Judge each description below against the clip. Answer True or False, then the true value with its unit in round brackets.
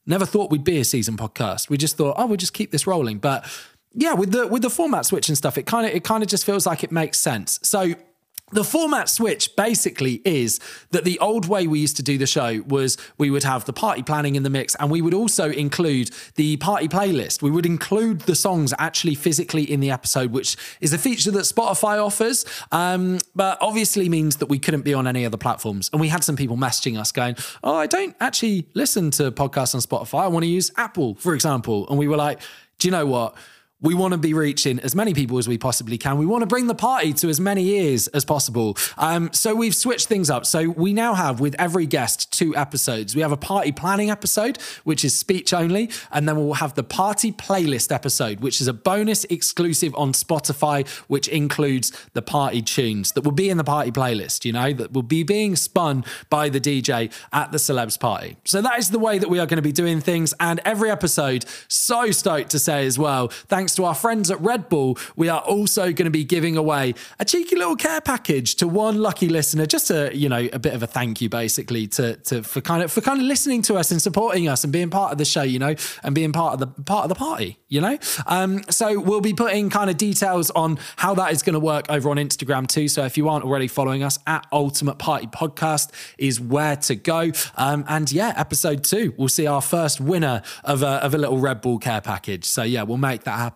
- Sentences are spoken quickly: True (240 wpm)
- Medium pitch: True (155 Hz)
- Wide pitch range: True (5.8 semitones)